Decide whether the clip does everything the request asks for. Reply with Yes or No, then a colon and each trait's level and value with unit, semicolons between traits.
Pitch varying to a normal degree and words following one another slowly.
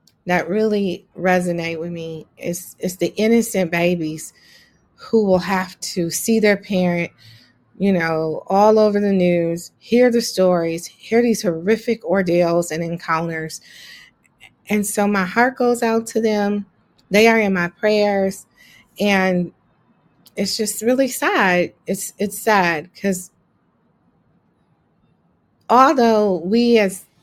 Yes: average, 3.7 semitones; slow, 125 wpm